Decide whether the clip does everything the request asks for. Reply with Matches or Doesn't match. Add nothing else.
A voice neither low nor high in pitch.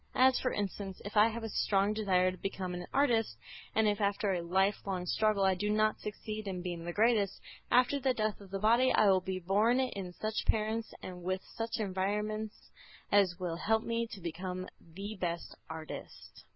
Doesn't match